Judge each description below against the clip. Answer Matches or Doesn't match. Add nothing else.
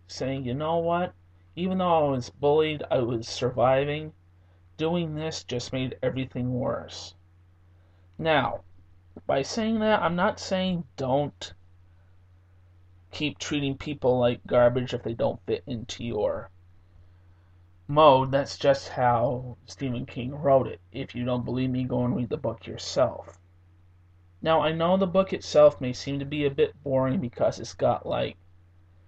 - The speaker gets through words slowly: Doesn't match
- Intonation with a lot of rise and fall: Matches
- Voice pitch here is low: Matches